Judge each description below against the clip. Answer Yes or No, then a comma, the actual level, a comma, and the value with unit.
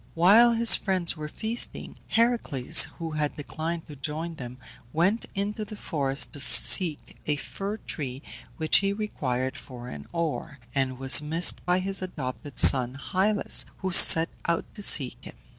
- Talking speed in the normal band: Yes, average, 160 wpm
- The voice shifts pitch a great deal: Yes, wide, 6.0 semitones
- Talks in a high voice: No, medium, 165 Hz